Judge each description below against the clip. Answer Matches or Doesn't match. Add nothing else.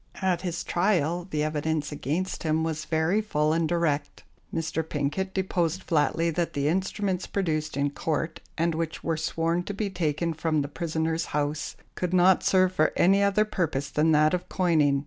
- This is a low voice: Doesn't match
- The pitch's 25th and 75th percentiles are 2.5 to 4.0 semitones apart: Matches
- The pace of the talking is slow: Doesn't match